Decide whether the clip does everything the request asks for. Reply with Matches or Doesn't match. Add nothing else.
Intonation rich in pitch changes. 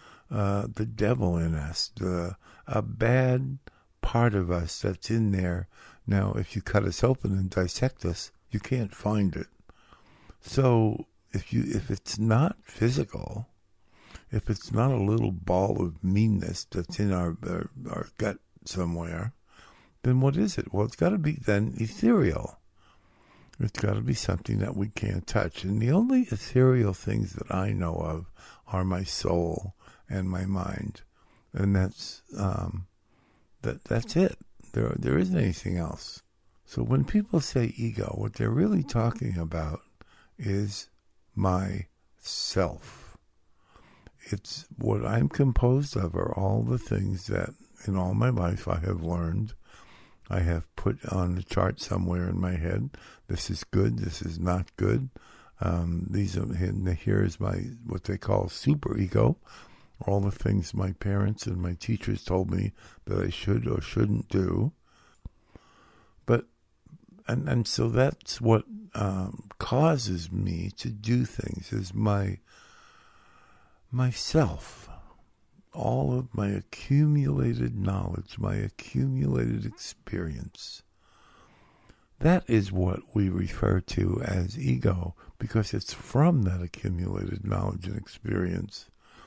Doesn't match